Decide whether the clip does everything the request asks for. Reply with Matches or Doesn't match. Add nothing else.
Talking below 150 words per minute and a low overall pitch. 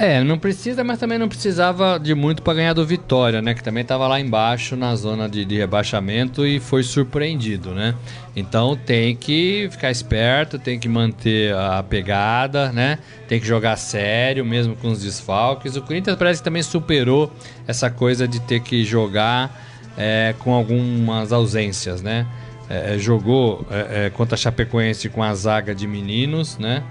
Doesn't match